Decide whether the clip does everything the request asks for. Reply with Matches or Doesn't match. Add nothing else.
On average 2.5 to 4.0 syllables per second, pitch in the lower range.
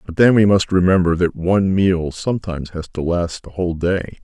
Doesn't match